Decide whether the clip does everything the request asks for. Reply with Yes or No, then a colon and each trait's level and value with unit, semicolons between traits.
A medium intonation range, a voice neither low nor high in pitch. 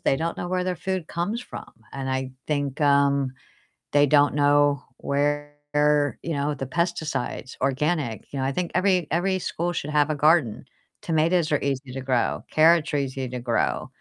Yes: average, 3.4 semitones; medium, 145 Hz